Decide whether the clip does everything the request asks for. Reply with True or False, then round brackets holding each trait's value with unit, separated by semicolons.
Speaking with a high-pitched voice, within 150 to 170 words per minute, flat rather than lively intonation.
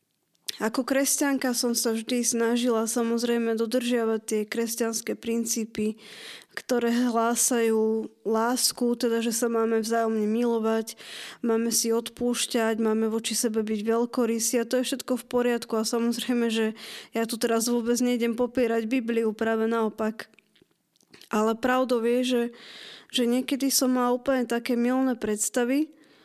False (235 Hz; 135 wpm; 1.5 semitones)